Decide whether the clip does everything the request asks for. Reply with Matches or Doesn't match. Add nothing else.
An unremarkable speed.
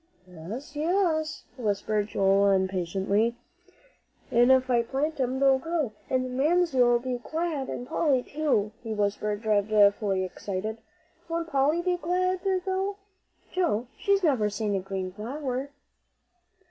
Doesn't match